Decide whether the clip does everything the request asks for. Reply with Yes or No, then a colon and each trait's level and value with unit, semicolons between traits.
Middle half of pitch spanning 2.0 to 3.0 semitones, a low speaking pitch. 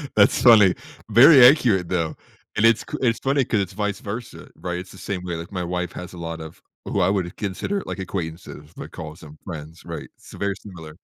No: average, 3.8 semitones; very low, 95 Hz